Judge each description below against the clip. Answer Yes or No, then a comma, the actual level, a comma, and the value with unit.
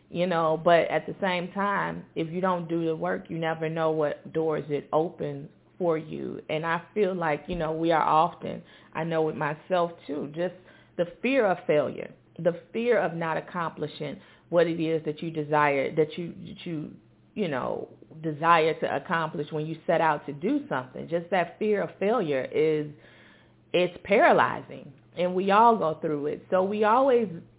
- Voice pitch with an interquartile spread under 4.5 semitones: Yes, narrow, 2.4 semitones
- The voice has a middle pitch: Yes, medium, 165 Hz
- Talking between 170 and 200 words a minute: Yes, average, 185 wpm